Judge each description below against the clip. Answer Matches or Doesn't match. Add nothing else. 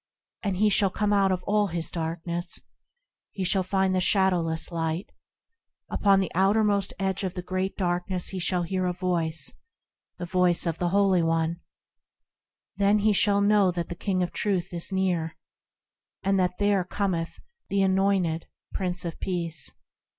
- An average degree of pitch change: Doesn't match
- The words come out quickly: Doesn't match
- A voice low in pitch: Doesn't match